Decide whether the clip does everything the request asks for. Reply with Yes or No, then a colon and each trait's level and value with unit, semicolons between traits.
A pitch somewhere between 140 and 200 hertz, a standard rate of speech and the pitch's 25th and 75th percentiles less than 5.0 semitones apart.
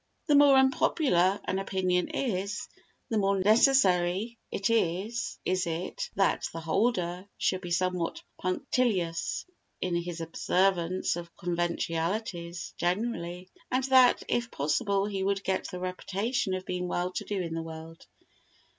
No: medium, 185 Hz; slow, 130 wpm; average, 3.5 semitones